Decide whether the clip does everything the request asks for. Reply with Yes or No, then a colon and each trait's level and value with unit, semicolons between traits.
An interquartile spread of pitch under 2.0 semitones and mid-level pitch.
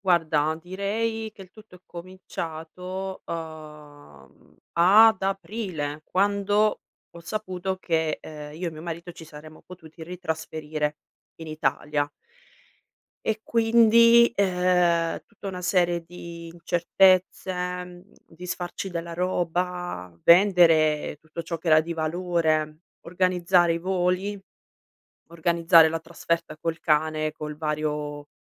No: average, 2.8 semitones; medium, 170 Hz